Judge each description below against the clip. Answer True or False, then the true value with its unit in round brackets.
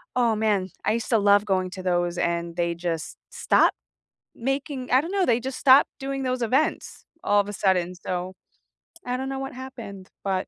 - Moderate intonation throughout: False (6.0 semitones)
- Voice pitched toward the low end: False (210 Hz)